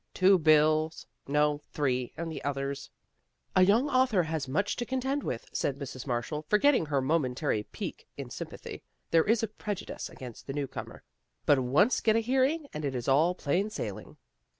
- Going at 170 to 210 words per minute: Yes, average, 185 wpm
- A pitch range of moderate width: No, wide, 7.2 semitones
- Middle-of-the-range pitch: Yes, medium, 155 Hz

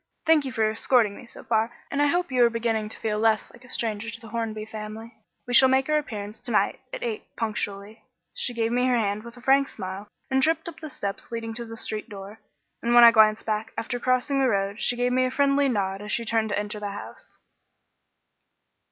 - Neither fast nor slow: No, fast, 240 wpm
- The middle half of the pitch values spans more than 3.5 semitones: No, average, 3.1 semitones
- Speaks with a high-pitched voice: Yes, high, 230 Hz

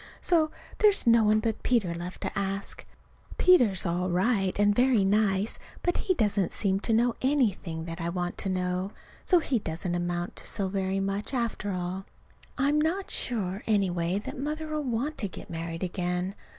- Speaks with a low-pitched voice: No, high, 200 Hz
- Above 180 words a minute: No, average, 175 wpm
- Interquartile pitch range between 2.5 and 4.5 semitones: No, average, 5.1 semitones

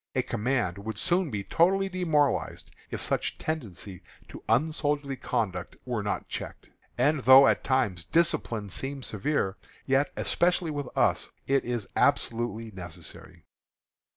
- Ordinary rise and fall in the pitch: No, wide, 5.9 semitones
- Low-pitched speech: Yes, low, 130 Hz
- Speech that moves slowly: Yes, slow, 130 wpm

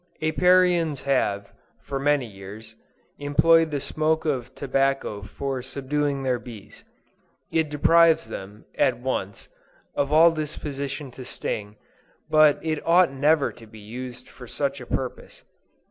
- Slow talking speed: Yes, slow, 130 wpm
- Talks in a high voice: No, medium, 140 Hz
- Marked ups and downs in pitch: No, average, 3.9 semitones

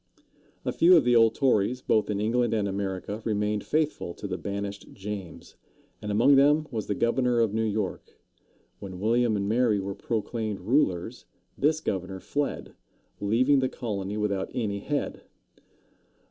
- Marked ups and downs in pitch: No, average, 3.6 semitones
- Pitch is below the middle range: Yes, low, 110 Hz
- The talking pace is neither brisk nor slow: Yes, average, 155 wpm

